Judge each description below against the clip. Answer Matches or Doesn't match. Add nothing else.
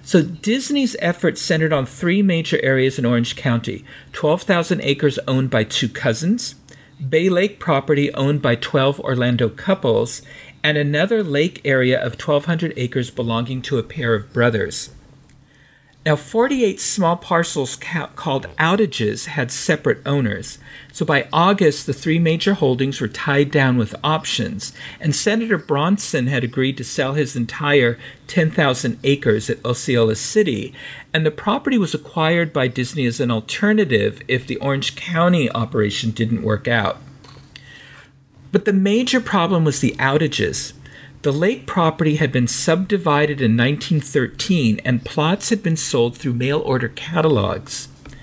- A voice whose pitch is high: Doesn't match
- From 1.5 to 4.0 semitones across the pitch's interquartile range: Doesn't match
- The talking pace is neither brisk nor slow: Matches